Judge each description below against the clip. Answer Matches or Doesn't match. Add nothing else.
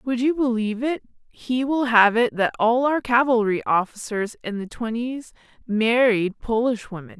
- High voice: Matches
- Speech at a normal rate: Matches